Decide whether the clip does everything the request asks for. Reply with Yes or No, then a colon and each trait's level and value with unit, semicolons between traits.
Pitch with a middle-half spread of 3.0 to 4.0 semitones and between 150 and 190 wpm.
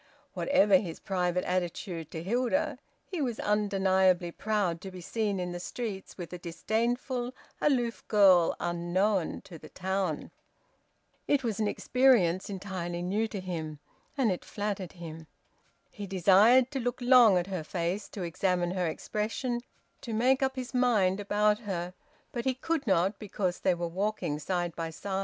No: average, 4.5 semitones; average, 160 wpm